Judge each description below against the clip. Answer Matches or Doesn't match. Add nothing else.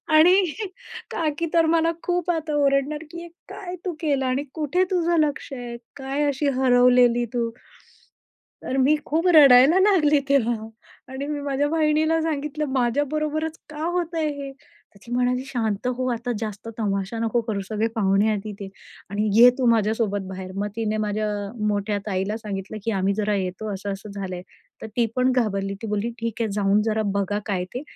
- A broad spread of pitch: Matches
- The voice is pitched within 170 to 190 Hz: Doesn't match